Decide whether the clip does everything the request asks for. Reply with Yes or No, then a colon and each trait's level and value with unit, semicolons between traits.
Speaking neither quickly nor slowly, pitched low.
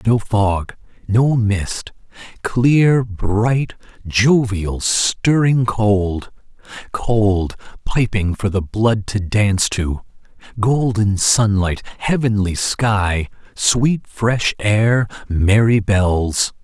No: slow, 95 wpm; low, 105 Hz